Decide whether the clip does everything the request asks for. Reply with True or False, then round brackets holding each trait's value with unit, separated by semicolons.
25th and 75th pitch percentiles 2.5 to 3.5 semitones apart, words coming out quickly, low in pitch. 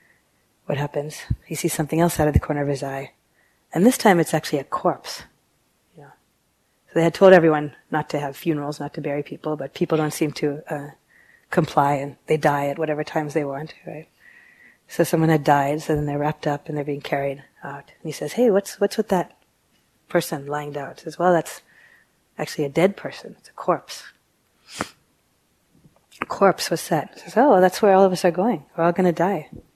False (3.0 semitones; 210 wpm; 155 Hz)